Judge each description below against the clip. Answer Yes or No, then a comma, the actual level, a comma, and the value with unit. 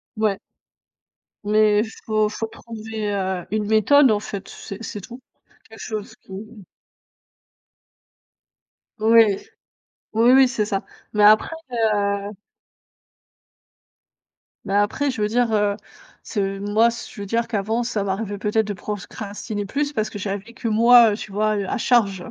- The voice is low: No, high, 215 Hz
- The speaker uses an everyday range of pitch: No, narrow, 2.0 semitones